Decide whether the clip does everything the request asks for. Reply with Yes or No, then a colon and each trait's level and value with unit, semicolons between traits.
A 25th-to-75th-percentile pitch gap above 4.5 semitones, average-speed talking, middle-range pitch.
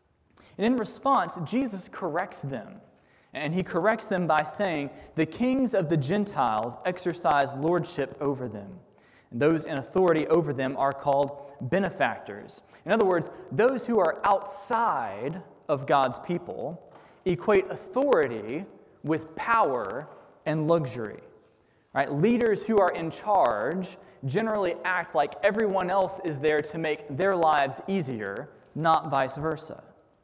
No: average, 5.2 semitones; slow, 130 wpm; medium, 175 Hz